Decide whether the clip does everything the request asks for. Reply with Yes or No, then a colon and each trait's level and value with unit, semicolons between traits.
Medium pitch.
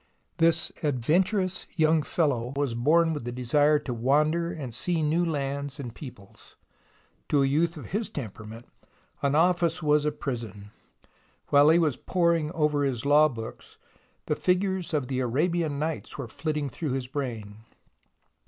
Yes: medium, 150 Hz